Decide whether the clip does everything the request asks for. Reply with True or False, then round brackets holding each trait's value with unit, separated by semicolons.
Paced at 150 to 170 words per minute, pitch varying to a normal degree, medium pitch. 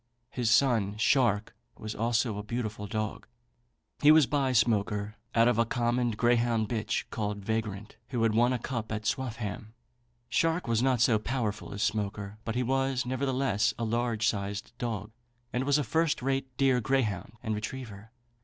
False (165 wpm; 3.0 semitones; 115 Hz)